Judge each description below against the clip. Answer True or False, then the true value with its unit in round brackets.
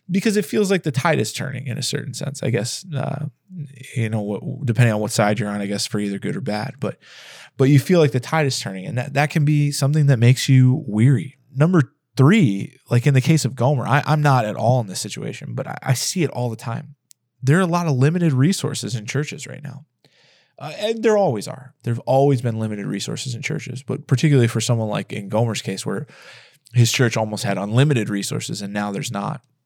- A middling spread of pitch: True (3.9 semitones)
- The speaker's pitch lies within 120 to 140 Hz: True (135 Hz)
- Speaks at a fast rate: True (235 wpm)